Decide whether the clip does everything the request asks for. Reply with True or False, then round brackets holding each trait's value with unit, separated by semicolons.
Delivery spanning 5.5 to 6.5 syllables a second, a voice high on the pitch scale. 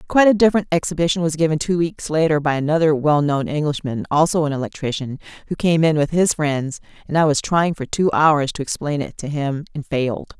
False (5.9 syllables/s; 155 Hz)